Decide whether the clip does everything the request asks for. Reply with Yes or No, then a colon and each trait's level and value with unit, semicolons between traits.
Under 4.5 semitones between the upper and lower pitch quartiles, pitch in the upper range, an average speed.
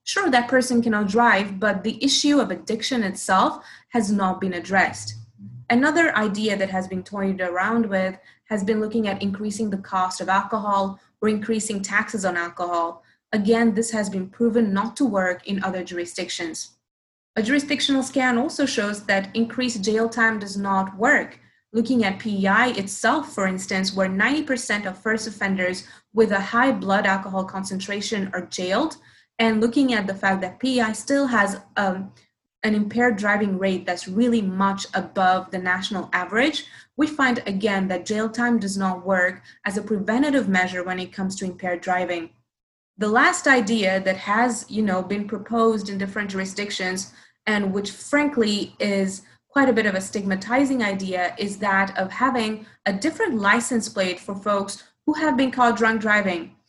Yes: average, 3.4 semitones; high, 205 Hz; average, 165 wpm